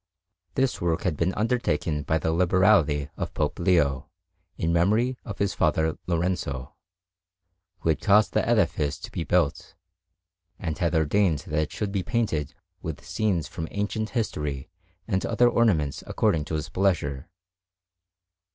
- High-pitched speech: No, very low, 85 Hz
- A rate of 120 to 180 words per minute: Yes, average, 145 wpm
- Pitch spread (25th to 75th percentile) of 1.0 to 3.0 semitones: No, average, 5.0 semitones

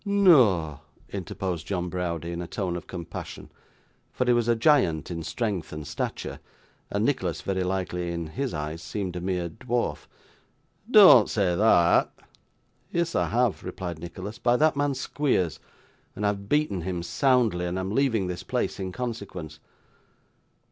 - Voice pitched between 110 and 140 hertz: No, very low, 95 Hz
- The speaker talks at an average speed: Yes, average, 155 wpm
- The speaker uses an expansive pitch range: Yes, wide, 5.8 semitones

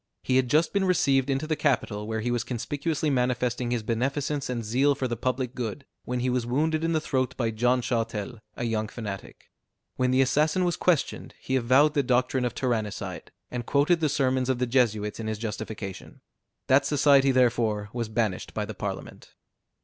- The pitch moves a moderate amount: Yes, average, 3.3 semitones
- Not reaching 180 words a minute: No, average, 190 wpm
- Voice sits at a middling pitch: No, low, 125 Hz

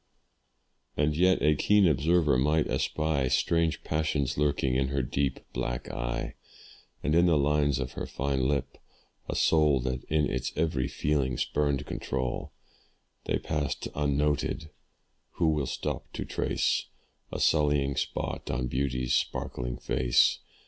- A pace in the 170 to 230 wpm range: No, slow, 135 wpm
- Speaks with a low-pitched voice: Yes, very low, 70 Hz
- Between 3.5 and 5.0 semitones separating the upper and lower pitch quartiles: No, average, 2.8 semitones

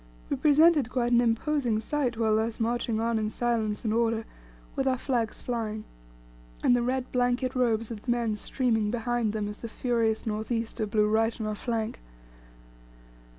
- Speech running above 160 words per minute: Yes, average, 175 wpm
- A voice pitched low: No, high, 230 Hz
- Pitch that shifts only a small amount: Yes, narrow, 2.0 semitones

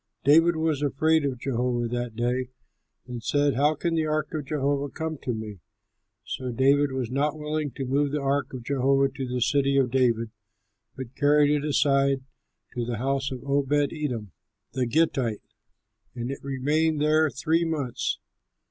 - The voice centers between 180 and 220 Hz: No, medium, 140 Hz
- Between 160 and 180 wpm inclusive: Yes, average, 165 wpm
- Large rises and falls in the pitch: No, average, 2.8 semitones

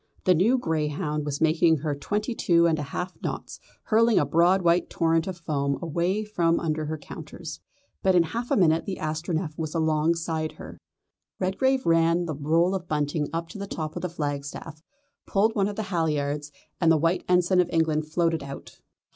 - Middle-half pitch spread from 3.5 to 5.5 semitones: No, average, 2.8 semitones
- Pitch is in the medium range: Yes, medium, 165 Hz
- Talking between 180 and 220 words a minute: Yes, average, 190 wpm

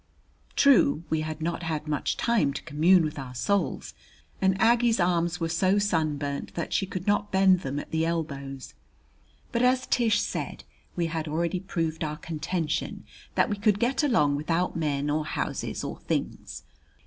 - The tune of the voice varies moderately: Yes, average, 4.1 semitones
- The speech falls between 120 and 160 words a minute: No, average, 170 wpm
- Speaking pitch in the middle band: Yes, medium, 165 Hz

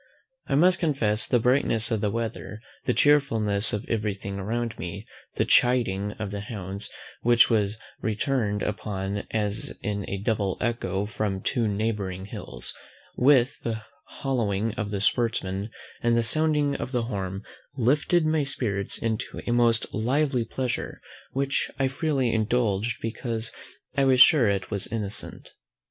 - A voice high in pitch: No, low, 110 Hz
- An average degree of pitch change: Yes, average, 3.6 semitones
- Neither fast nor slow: Yes, average, 150 wpm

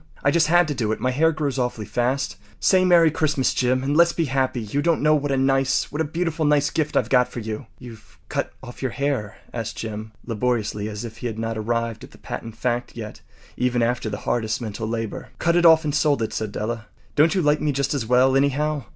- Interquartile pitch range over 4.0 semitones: Yes, average, 4.6 semitones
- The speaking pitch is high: No, low, 130 Hz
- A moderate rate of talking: No, fast, 235 wpm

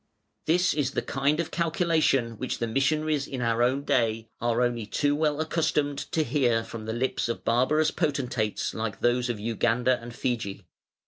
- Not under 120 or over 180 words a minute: Yes, average, 175 wpm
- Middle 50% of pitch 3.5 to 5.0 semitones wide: Yes, average, 4.3 semitones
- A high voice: No, low, 125 Hz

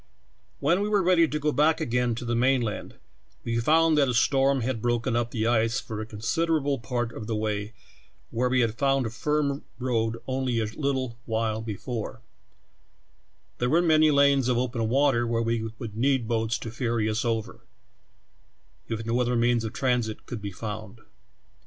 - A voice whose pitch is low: Yes, low, 120 Hz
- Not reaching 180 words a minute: No, average, 185 wpm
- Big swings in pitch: No, average, 3.3 semitones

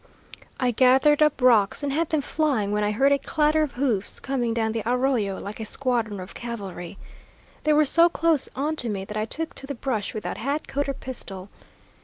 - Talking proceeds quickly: Yes, fast, 210 wpm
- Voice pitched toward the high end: Yes, very high, 255 Hz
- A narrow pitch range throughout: No, average, 5.1 semitones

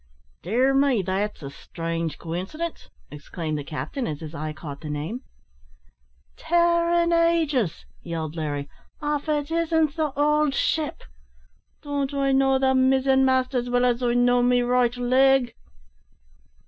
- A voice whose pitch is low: No, very high, 255 Hz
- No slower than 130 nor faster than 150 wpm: Yes, average, 145 wpm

